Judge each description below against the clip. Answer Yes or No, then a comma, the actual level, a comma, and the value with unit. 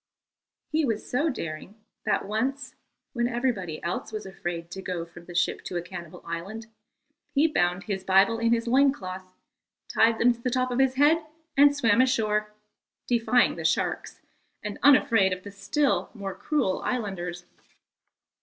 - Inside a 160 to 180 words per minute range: Yes, average, 165 wpm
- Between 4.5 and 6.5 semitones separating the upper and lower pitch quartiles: Yes, wide, 5.5 semitones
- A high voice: Yes, high, 220 Hz